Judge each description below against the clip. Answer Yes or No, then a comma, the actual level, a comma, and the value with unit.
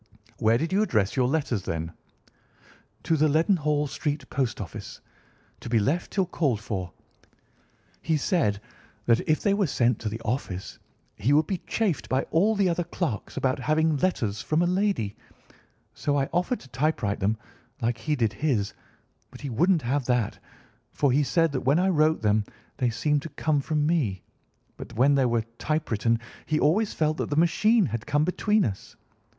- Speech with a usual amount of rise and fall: No, wide, 6.0 semitones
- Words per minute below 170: No, average, 180 wpm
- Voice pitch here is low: No, medium, 145 Hz